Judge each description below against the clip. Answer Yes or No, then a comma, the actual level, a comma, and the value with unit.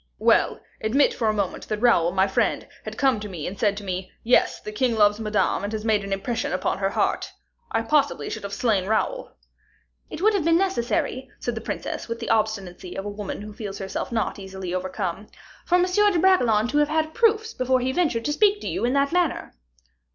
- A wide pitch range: Yes, wide, 6.6 semitones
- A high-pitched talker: Yes, high, 225 Hz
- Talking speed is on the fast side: Yes, fast, 215 wpm